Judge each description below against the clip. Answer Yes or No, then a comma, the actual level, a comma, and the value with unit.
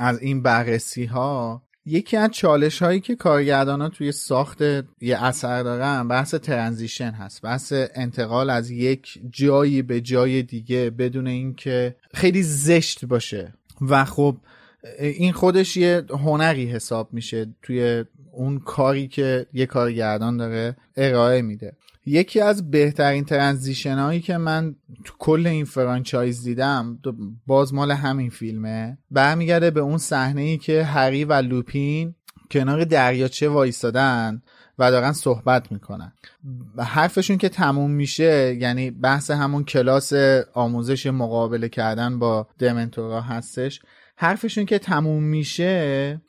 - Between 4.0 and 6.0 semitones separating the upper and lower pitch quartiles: No, average, 3.5 semitones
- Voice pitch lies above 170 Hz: No, low, 135 Hz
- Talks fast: No, average, 125 wpm